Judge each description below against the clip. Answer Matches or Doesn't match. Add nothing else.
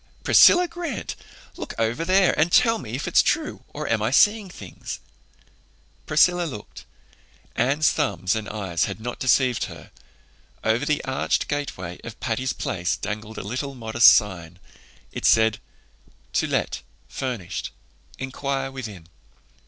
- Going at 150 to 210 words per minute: Doesn't match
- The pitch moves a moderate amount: Doesn't match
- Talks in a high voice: Doesn't match